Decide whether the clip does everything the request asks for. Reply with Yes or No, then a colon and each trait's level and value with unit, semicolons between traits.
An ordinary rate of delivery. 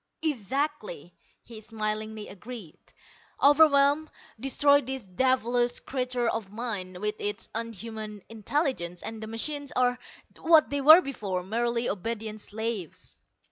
No: slow, 115 wpm